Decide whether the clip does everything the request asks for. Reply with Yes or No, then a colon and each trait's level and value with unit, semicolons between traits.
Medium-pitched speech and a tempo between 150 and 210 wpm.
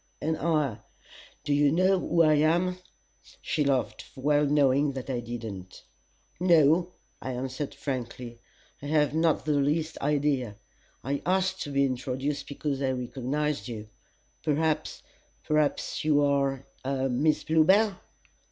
No: medium, 145 Hz; slow, 135 wpm